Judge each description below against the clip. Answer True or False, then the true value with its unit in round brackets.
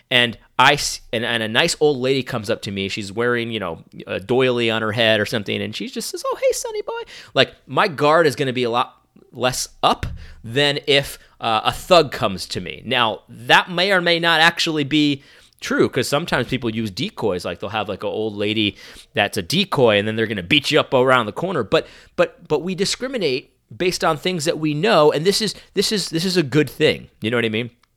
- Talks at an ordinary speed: False (240 wpm)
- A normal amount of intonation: False (7.1 semitones)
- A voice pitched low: False (145 Hz)